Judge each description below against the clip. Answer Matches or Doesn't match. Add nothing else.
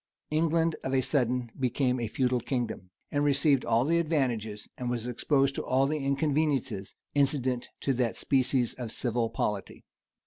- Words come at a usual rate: Matches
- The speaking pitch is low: Matches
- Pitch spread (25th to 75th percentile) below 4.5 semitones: Matches